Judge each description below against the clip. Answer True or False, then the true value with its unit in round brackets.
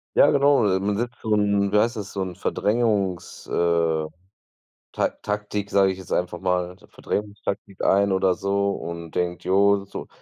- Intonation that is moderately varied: False (2.3 semitones)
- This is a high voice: False (100 Hz)